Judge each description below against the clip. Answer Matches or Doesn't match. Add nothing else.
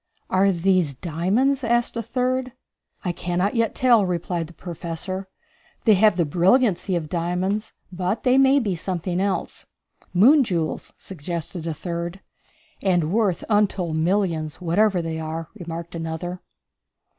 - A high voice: Doesn't match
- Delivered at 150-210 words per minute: Doesn't match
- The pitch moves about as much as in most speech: Matches